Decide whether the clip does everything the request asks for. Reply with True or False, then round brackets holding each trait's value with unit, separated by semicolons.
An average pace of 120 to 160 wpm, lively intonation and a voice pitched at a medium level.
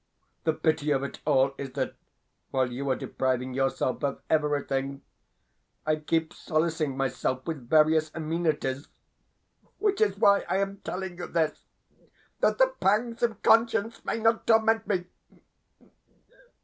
True (135 wpm; 6.4 semitones; 155 Hz)